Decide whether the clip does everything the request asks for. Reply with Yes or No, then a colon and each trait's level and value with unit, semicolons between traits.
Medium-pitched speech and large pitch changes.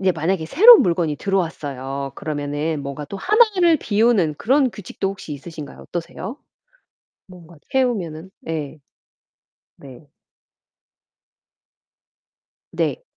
Yes: medium, 170 Hz; wide, 6.6 semitones